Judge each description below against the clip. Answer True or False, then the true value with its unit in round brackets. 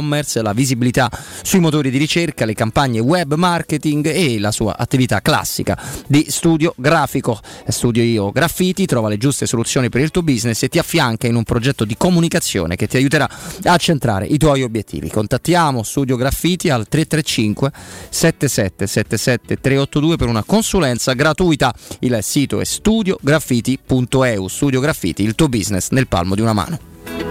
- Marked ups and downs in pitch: True (5.7 semitones)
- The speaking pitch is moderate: False (130 Hz)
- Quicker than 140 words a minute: True (150 wpm)